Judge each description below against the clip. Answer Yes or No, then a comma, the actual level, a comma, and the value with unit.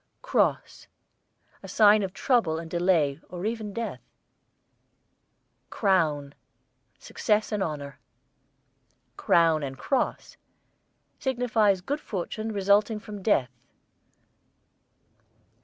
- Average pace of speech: No, slow, 90 wpm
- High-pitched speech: Yes, high, 200 Hz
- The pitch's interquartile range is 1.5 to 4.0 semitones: No, average, 5.0 semitones